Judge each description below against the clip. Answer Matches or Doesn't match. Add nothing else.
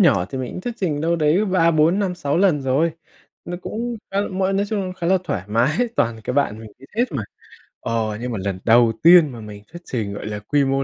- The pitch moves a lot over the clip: Matches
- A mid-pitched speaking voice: Matches